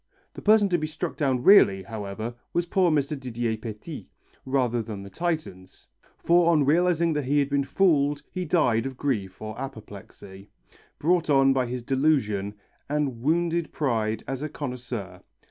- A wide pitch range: Yes, wide, 5.9 semitones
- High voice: No, low, 135 Hz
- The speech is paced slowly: No, average, 165 wpm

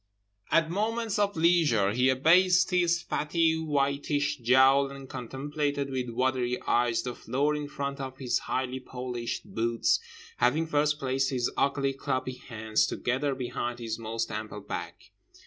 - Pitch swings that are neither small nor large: Yes, average, 3.4 semitones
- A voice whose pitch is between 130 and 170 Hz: Yes, low, 135 Hz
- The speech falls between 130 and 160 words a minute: Yes, average, 145 wpm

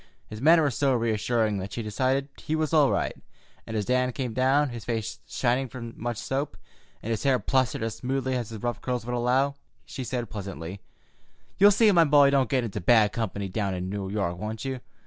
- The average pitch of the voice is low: Yes, low, 120 Hz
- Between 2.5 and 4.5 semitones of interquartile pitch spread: Yes, average, 3.8 semitones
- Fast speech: Yes, fast, 210 wpm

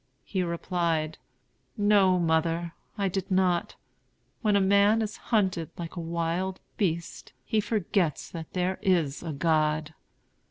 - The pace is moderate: No, slow, 130 wpm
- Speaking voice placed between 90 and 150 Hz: No, medium, 175 Hz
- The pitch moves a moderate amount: Yes, average, 3.0 semitones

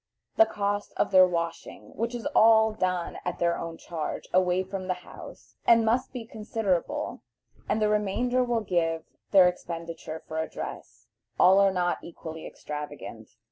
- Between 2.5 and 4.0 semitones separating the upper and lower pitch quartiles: No, average, 4.4 semitones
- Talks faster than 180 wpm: No, average, 155 wpm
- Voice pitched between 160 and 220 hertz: Yes, medium, 185 Hz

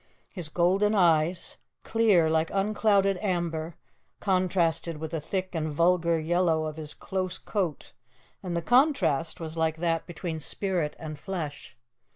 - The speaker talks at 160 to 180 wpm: No, average, 140 wpm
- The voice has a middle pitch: Yes, medium, 170 Hz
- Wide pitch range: No, average, 2.9 semitones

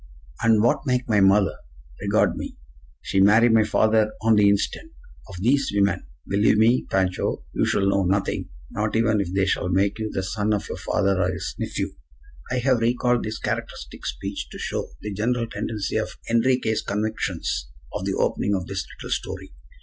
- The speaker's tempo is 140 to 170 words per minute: No, average, 180 wpm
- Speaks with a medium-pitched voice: No, low, 105 Hz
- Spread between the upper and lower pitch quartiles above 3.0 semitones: No, average, 2.7 semitones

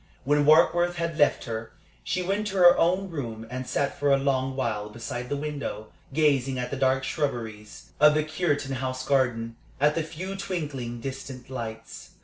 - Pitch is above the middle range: No, low, 135 Hz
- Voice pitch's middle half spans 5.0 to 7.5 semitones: No, average, 3.8 semitones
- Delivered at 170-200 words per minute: Yes, average, 175 wpm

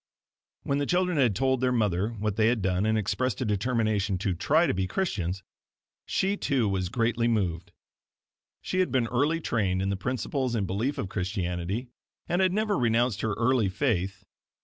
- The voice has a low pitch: Yes, low, 115 Hz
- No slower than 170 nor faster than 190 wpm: Yes, average, 180 wpm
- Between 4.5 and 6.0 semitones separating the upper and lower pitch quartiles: Yes, average, 5.2 semitones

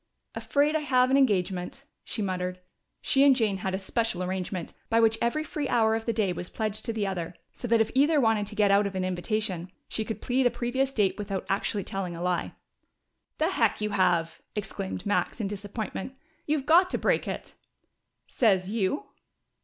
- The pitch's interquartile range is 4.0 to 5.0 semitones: Yes, average, 4.5 semitones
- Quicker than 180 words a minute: Yes, average, 195 wpm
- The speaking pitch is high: Yes, high, 215 Hz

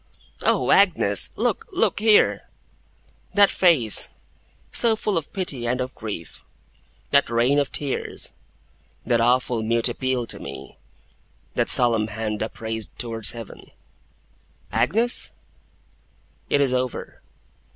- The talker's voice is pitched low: Yes, low, 125 Hz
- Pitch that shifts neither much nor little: Yes, average, 4.3 semitones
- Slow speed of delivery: Yes, slow, 115 wpm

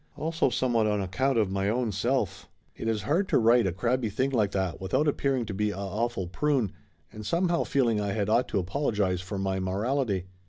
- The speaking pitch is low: Yes, low, 110 Hz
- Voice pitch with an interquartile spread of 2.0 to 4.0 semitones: No, average, 4.8 semitones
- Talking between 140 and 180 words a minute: No, fast, 205 wpm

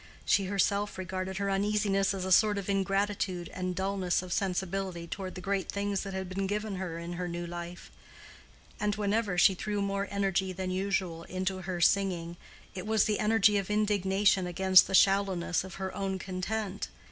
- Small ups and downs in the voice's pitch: Yes, narrow, 1.5 semitones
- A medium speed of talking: Yes, average, 180 wpm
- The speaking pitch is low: No, high, 195 Hz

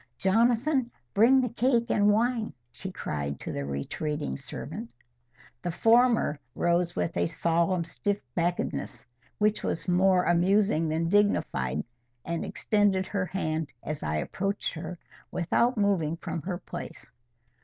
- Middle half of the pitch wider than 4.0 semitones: Yes, average, 4.7 semitones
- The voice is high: No, medium, 180 Hz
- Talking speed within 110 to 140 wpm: Yes, slow, 135 wpm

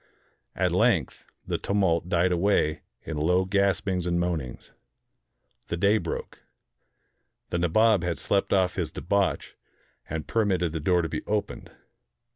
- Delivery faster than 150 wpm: No, average, 140 wpm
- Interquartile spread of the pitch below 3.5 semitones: Yes, average, 2.9 semitones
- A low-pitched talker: Yes, very low, 90 Hz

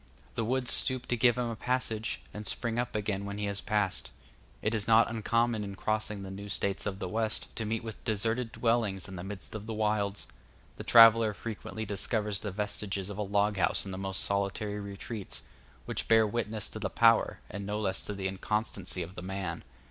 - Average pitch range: No, narrow, 2.2 semitones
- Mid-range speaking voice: No, low, 105 Hz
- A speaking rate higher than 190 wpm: Yes, fast, 205 wpm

